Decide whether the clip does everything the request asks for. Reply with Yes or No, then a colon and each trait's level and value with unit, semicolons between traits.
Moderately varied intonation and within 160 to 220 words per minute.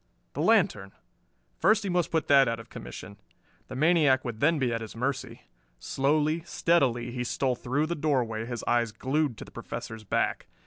Yes: average, 4.8 semitones; average, 180 wpm